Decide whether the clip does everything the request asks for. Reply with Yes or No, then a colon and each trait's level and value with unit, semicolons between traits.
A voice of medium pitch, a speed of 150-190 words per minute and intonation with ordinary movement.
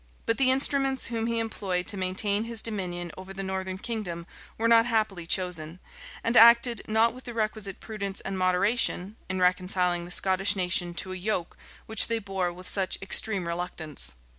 No: high, 195 Hz; average, 175 wpm; average, 3.7 semitones